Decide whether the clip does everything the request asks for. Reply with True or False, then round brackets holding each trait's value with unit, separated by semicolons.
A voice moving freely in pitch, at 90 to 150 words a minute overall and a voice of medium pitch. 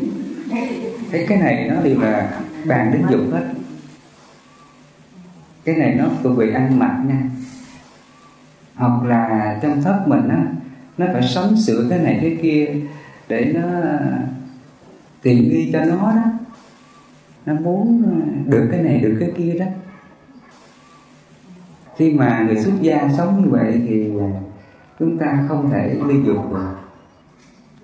True (6.1 semitones; 140 wpm; 150 Hz)